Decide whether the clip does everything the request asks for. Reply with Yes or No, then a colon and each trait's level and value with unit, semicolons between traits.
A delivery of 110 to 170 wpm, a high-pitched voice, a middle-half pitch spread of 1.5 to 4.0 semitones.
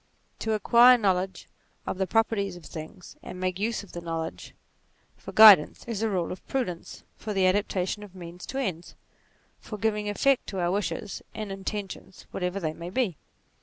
No: average, 180 wpm; high, 195 Hz; average, 3.1 semitones